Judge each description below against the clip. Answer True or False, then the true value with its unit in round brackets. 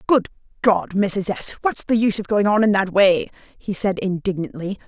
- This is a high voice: True (200 Hz)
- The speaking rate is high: False (195 wpm)